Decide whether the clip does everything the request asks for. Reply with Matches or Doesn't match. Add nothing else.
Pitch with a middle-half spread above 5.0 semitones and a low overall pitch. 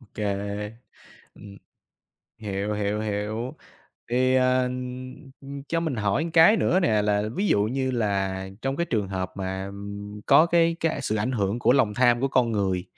Doesn't match